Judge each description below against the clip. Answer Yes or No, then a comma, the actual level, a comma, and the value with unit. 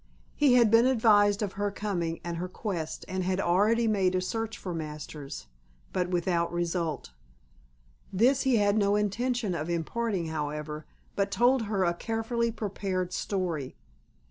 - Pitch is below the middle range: No, high, 195 Hz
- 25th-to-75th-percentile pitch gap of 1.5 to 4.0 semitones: No, average, 4.5 semitones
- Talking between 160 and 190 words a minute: No, average, 150 wpm